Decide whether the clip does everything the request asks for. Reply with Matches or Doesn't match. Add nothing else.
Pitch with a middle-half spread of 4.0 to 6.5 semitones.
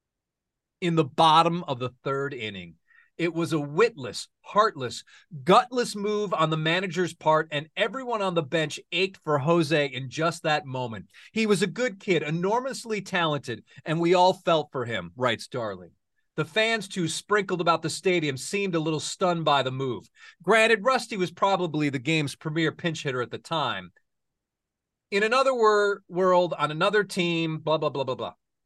Matches